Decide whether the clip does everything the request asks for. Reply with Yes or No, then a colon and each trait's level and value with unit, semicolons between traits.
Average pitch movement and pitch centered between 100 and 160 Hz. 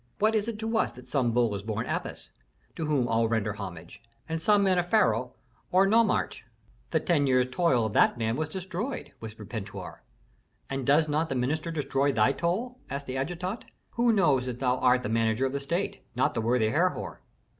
No: wide, 7.4 semitones; low, 135 Hz